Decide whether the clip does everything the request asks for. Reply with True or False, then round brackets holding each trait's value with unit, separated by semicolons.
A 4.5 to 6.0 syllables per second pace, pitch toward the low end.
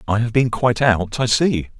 True (5.1 syllables/s; 115 Hz)